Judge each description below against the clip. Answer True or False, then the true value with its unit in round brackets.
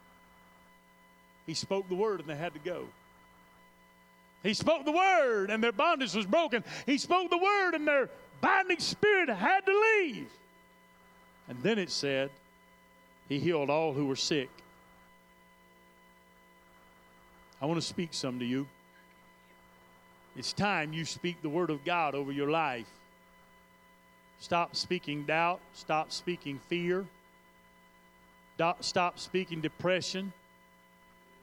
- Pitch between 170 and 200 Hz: False (140 Hz)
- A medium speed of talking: False (125 wpm)